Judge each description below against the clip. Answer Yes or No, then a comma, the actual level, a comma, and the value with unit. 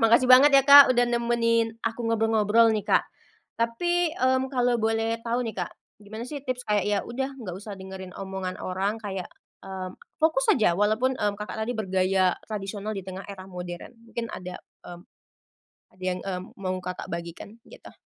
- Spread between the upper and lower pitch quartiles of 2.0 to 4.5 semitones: Yes, average, 3.9 semitones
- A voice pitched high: Yes, high, 220 Hz